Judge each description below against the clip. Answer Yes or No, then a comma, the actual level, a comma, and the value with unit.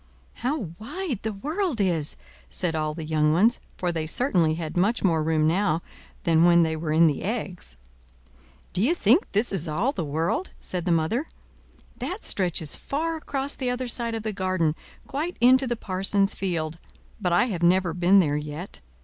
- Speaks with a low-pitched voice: No, medium, 185 Hz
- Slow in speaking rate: No, average, 180 wpm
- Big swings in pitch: Yes, wide, 6.8 semitones